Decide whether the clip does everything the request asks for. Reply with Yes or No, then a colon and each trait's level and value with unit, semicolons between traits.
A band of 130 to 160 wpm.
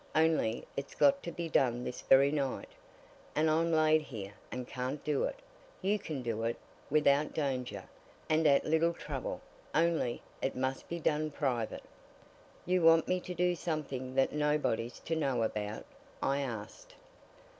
Yes: average, 155 wpm